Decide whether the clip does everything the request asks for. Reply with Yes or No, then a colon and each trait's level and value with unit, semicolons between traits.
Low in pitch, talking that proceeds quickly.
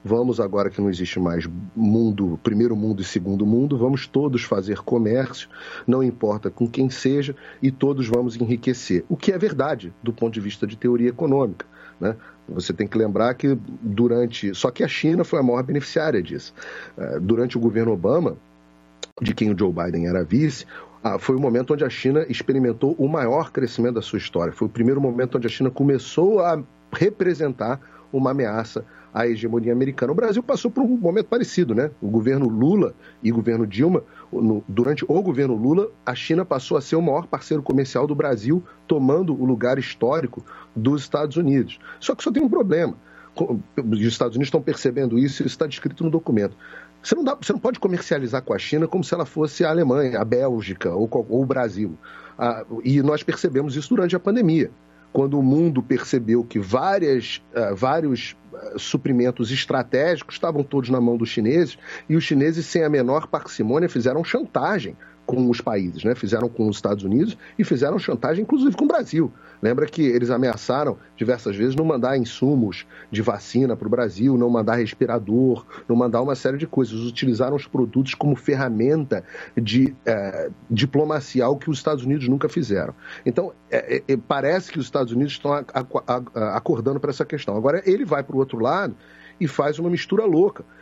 Yes: low, 130 Hz; fast, 190 wpm